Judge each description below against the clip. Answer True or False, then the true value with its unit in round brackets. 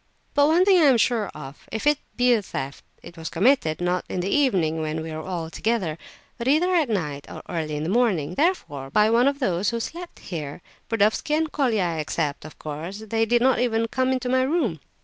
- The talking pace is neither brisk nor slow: False (225 wpm)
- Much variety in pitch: True (8.2 semitones)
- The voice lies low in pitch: False (215 Hz)